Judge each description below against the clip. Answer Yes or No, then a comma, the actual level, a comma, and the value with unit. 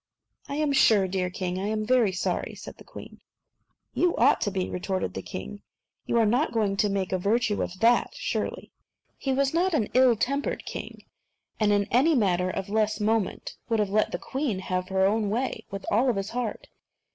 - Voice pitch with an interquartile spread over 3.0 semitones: Yes, average, 4.3 semitones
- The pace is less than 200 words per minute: No, fast, 205 wpm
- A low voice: No, high, 215 Hz